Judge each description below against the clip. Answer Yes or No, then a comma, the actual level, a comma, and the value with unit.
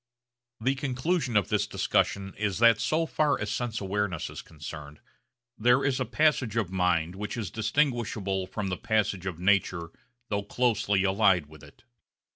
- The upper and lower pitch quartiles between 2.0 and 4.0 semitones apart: No, average, 4.7 semitones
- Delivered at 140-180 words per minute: Yes, average, 160 wpm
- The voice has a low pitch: Yes, low, 105 Hz